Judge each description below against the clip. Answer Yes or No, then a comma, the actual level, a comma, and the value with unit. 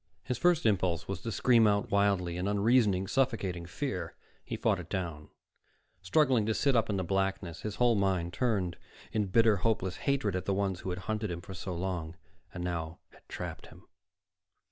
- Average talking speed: Yes, average, 190 wpm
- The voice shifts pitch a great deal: No, average, 3.8 semitones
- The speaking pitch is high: No, very low, 95 Hz